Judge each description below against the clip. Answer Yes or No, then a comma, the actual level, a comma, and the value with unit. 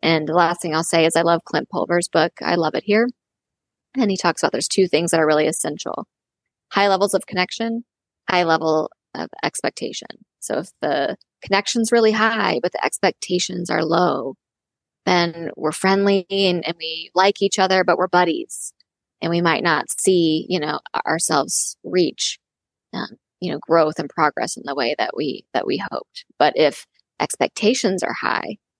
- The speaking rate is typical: Yes, average, 180 wpm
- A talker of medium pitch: Yes, medium, 180 Hz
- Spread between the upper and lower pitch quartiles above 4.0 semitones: No, average, 3.3 semitones